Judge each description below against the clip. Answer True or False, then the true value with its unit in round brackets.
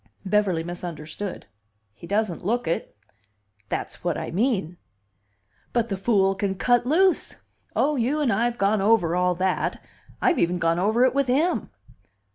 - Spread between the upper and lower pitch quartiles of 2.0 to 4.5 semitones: False (5.2 semitones)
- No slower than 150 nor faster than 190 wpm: True (155 wpm)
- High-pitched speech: True (200 Hz)